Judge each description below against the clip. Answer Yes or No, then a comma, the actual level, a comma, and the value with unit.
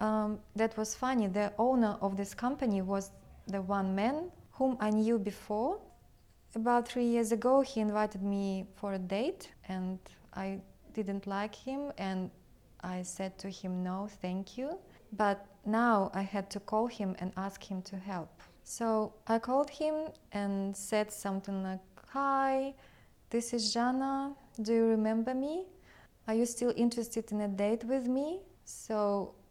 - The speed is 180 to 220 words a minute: No, average, 160 wpm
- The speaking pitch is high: Yes, high, 215 Hz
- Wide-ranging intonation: No, average, 3.6 semitones